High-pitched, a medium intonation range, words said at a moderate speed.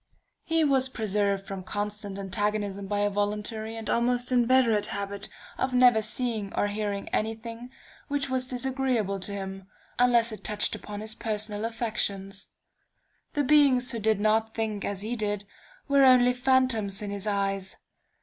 Yes: high, 215 Hz; average, 3.4 semitones; average, 155 wpm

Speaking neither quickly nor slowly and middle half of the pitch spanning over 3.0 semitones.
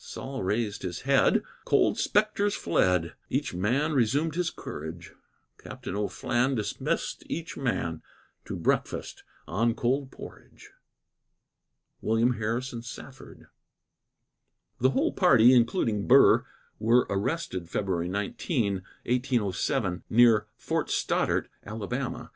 No: slow, 105 wpm; average, 5.0 semitones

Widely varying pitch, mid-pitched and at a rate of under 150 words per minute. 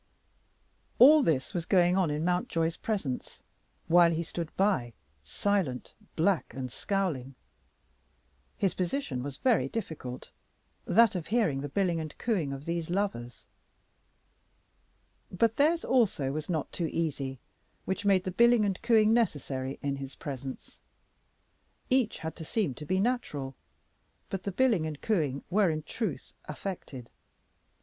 Yes: wide, 6.5 semitones; medium, 170 Hz; average, 140 wpm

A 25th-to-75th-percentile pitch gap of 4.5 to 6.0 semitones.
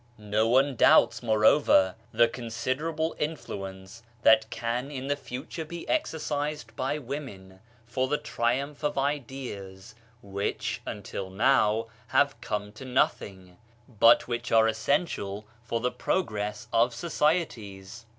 Yes: average, 5.0 semitones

